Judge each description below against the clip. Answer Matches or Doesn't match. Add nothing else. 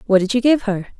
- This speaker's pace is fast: Matches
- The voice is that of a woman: Matches